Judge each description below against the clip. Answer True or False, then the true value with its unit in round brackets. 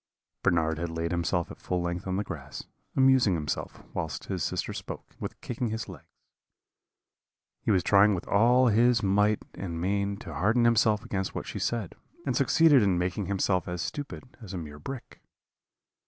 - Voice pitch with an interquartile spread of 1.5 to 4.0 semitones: False (4.8 semitones)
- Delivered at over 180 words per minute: False (175 wpm)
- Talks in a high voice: False (100 Hz)